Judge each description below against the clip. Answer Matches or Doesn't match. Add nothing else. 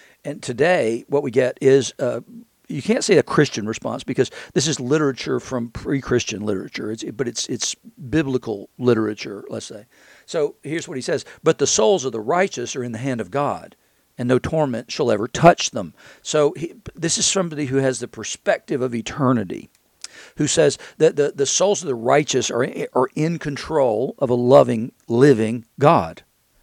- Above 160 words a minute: Matches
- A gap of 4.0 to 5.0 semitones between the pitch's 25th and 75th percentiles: Matches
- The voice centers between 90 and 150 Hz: Matches